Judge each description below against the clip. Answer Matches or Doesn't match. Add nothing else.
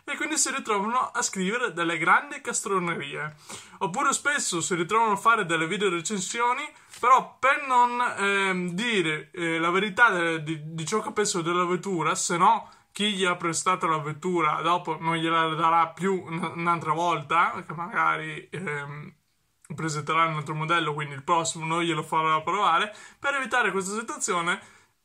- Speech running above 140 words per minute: Matches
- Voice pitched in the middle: Matches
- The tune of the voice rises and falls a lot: Doesn't match